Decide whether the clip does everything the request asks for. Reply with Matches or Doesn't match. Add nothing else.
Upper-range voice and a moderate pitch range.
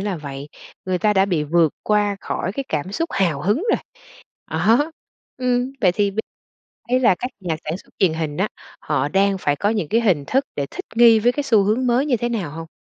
Doesn't match